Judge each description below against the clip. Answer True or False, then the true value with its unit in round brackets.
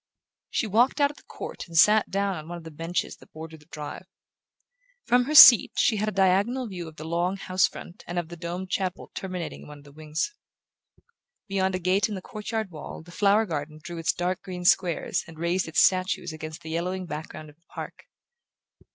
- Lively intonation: False (3.5 semitones)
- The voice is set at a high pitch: False (180 Hz)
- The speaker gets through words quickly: True (215 wpm)